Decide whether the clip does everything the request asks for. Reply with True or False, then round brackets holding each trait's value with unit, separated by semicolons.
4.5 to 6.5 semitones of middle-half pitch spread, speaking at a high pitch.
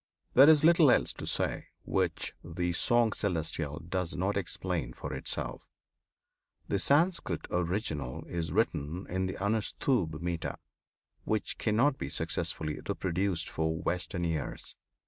False (4.8 semitones; 90 Hz)